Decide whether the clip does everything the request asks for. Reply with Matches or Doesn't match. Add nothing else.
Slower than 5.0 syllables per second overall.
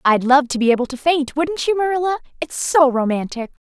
Doesn't match